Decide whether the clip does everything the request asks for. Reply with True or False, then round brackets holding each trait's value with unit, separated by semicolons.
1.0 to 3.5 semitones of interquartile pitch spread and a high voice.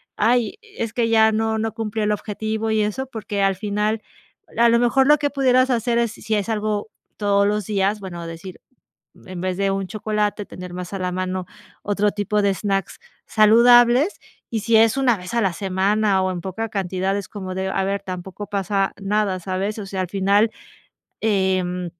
True (2.6 semitones; 205 Hz)